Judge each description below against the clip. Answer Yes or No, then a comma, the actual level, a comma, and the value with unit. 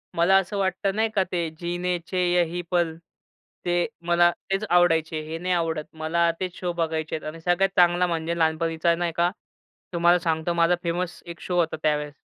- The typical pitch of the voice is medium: Yes, medium, 170 Hz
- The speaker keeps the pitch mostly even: Yes, narrow, 1.5 semitones